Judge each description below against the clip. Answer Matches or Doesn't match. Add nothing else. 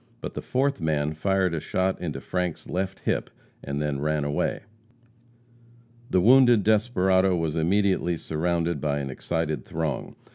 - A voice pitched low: Matches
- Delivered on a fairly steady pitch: Doesn't match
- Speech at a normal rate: Matches